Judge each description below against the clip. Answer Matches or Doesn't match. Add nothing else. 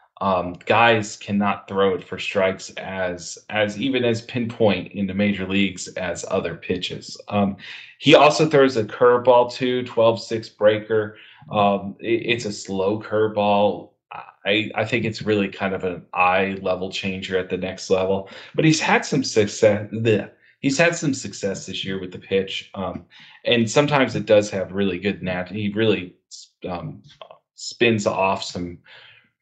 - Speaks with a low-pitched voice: Matches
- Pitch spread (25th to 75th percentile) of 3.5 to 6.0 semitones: Doesn't match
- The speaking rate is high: Doesn't match